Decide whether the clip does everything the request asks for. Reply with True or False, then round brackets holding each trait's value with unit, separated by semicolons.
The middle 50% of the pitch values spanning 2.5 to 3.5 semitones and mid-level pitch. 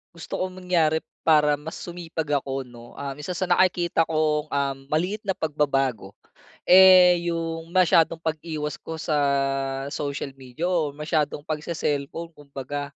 True (2.8 semitones; 155 Hz)